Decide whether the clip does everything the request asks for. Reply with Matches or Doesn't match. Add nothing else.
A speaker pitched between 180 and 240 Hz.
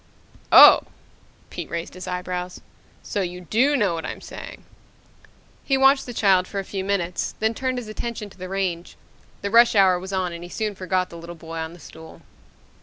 Matches